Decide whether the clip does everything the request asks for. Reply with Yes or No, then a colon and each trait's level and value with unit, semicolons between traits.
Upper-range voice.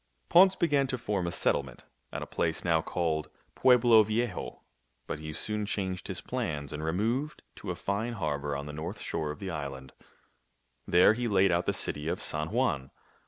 No: very low, 90 Hz